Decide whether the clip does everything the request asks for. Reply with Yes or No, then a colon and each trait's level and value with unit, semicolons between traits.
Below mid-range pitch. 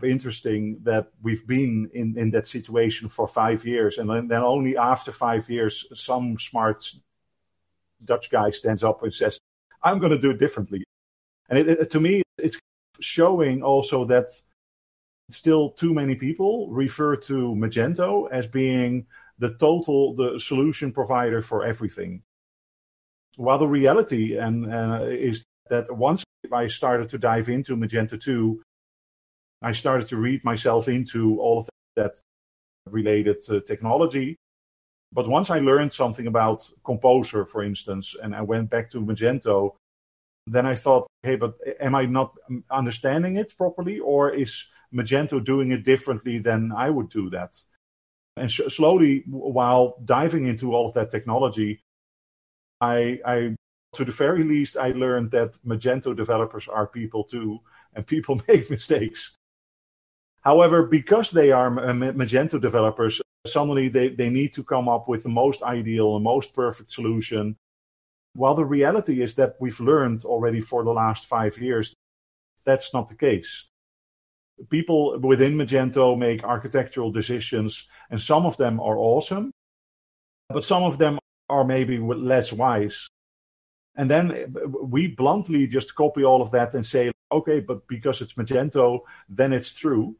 Yes: low, 125 Hz